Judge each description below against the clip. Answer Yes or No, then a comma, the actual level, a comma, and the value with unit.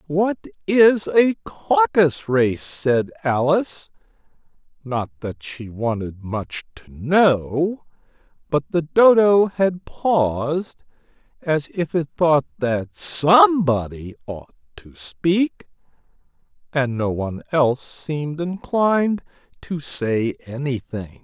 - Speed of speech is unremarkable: No, slow, 105 wpm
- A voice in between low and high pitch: Yes, medium, 150 Hz